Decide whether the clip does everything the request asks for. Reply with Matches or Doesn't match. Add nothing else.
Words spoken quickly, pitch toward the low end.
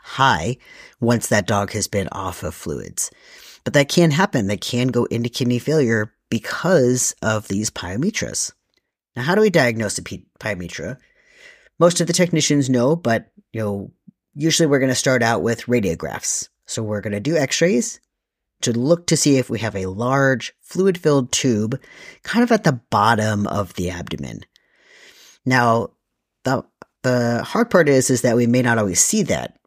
Doesn't match